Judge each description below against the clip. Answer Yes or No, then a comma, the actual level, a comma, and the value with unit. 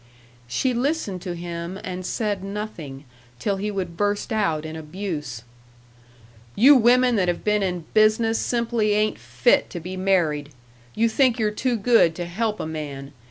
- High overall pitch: Yes, high, 195 Hz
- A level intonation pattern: No, average, 4.6 semitones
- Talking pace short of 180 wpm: Yes, average, 160 wpm